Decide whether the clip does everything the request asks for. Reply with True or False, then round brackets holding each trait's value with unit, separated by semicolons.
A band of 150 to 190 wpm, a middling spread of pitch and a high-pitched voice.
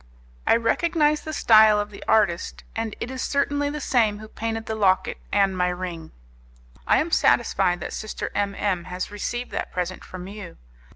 True (180 wpm; 3.8 semitones; 210 Hz)